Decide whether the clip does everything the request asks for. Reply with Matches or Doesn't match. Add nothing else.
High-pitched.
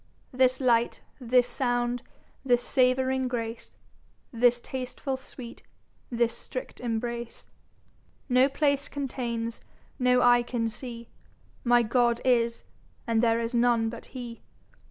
Matches